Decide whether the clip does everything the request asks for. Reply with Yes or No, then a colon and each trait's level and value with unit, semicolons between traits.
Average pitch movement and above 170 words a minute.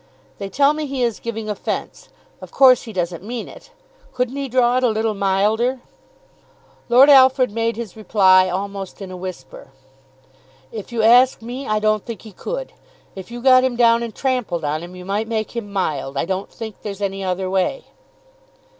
Yes: average, 4.3 semitones; average, 190 wpm